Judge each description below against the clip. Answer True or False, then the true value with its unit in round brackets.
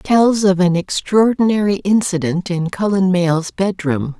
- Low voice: False (190 Hz)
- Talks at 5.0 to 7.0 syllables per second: False (4.3 syllables/s)